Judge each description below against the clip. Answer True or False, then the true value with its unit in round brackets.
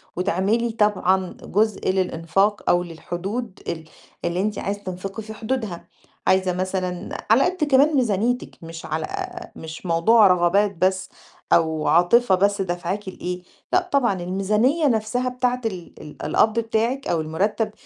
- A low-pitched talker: False (195 Hz)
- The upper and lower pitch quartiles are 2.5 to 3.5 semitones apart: False (4.1 semitones)